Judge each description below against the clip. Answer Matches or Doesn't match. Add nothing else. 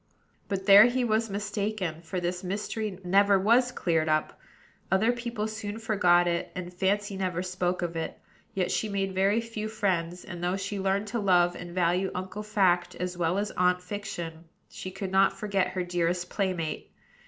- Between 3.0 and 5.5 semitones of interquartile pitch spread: Doesn't match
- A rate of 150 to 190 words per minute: Matches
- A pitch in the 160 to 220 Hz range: Matches